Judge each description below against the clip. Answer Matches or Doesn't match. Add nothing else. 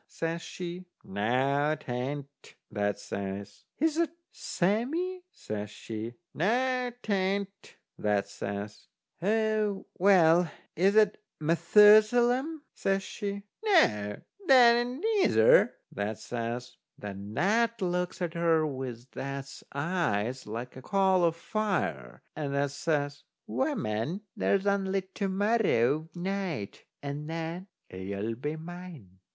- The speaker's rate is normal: Doesn't match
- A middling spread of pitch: Doesn't match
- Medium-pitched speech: Matches